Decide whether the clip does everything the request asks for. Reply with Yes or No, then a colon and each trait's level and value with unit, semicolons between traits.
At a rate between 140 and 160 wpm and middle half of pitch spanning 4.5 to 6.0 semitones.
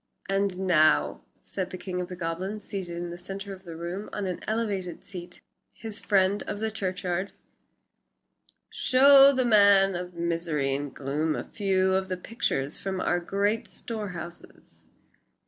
No: average, 155 wpm; average, 2.7 semitones